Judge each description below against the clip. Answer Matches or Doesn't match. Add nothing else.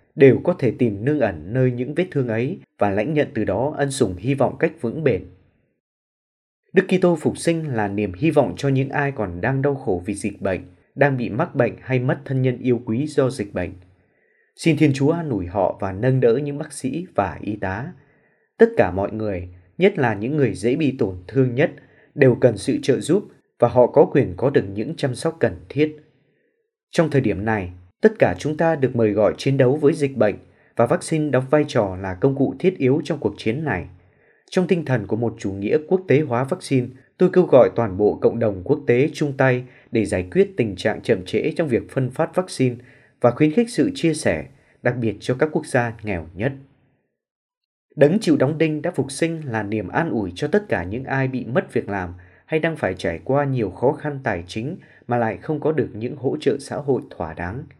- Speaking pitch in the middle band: Doesn't match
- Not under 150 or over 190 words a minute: Doesn't match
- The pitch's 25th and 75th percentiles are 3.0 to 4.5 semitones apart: Doesn't match